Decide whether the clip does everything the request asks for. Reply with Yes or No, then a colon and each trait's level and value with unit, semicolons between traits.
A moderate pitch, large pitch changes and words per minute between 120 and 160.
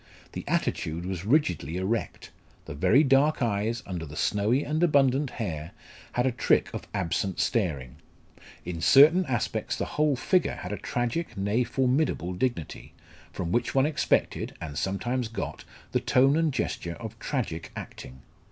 No: low, 115 Hz; wide, 7.2 semitones; average, 150 wpm